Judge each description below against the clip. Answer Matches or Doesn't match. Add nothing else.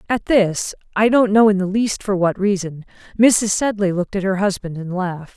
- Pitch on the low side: Doesn't match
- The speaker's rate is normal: Doesn't match